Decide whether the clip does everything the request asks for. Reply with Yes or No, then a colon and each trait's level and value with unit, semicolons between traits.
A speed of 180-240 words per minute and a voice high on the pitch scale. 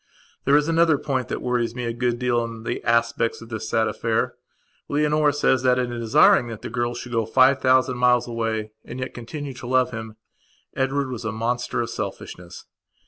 No: average, 195 wpm; low, 120 Hz